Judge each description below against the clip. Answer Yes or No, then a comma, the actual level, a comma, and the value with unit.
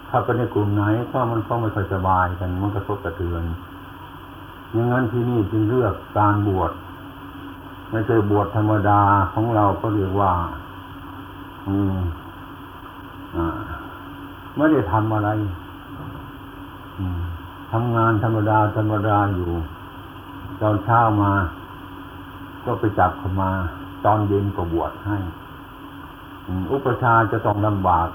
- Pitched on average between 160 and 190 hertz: No, low, 100 Hz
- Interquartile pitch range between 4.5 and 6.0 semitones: No, average, 2.7 semitones